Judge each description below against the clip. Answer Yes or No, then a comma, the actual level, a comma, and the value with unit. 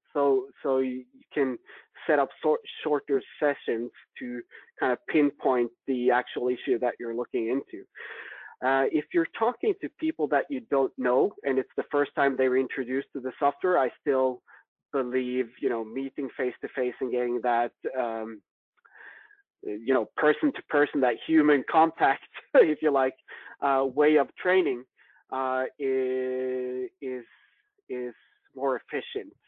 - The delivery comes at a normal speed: Yes, average, 155 wpm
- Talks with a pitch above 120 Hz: Yes, low, 135 Hz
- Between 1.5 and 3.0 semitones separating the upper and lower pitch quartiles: Yes, narrow, 2.6 semitones